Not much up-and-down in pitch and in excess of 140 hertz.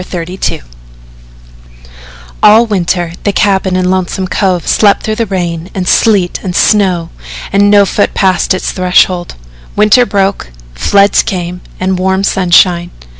Yes: narrow, 2.0 semitones; medium, 185 Hz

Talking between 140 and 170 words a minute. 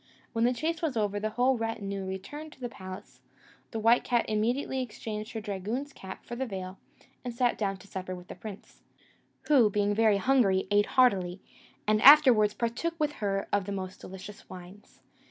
No: average, 185 wpm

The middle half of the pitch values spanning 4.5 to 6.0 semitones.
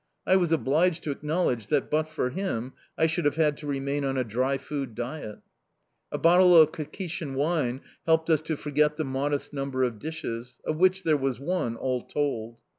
No: average, 3.4 semitones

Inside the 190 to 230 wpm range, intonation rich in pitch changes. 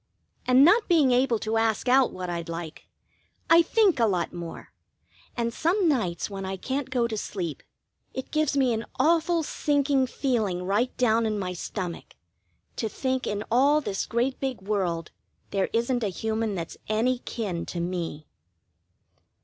No: average, 165 wpm; wide, 5.8 semitones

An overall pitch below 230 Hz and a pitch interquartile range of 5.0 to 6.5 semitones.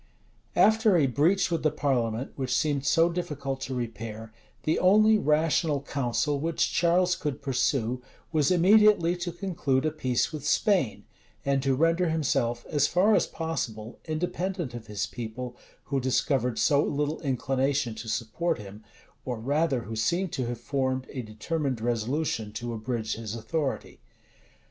Yes: medium, 140 Hz; wide, 5.4 semitones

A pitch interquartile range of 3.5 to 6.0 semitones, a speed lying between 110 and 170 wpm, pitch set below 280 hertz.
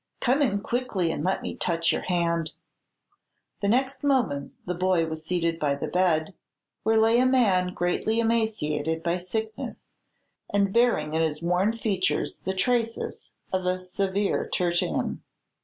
Yes: average, 4.8 semitones; average, 150 wpm; medium, 185 Hz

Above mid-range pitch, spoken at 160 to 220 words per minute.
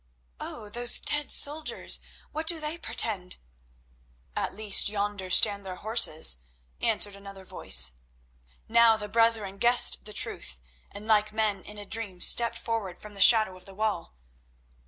No: high, 210 Hz; average, 145 wpm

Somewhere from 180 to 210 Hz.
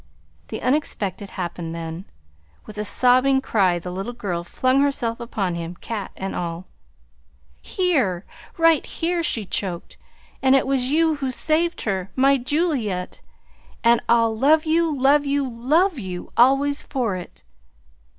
No: high, 245 Hz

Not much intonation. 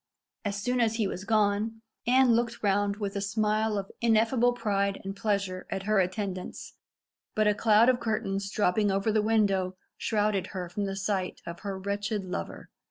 Yes: narrow, 2.0 semitones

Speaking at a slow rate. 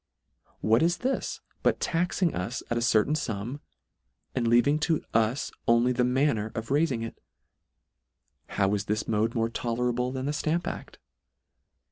No: average, 150 wpm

